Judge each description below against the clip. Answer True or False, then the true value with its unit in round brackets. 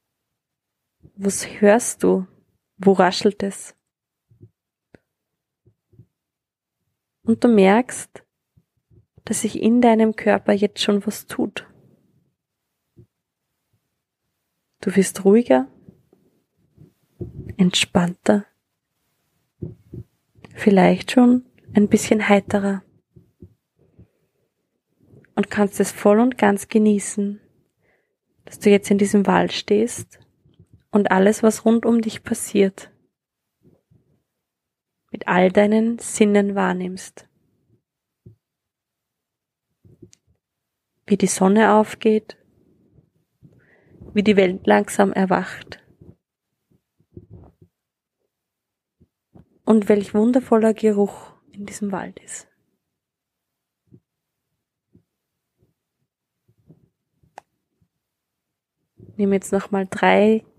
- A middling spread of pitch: False (1.9 semitones)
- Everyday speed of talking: False (75 wpm)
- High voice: True (205 Hz)